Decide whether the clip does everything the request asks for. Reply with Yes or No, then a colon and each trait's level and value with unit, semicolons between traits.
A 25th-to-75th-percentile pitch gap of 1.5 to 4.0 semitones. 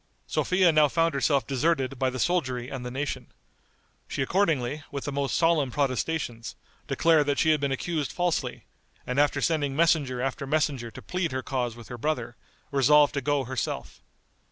Yes: average, 3.3 semitones